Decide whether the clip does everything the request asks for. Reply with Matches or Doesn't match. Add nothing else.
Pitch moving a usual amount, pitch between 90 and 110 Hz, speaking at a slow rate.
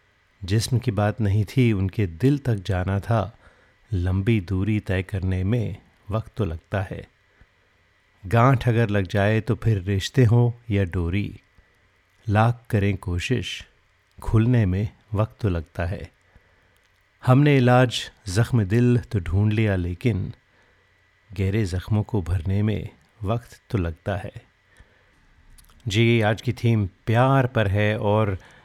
Matches